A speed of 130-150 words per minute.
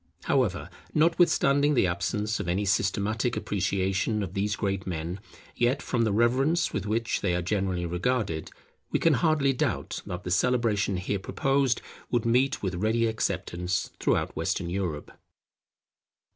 Yes: average, 145 wpm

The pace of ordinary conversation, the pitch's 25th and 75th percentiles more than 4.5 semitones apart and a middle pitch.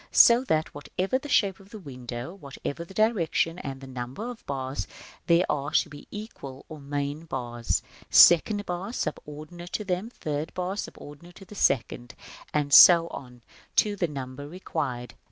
Yes: average, 165 wpm; wide, 5.5 semitones; medium, 155 Hz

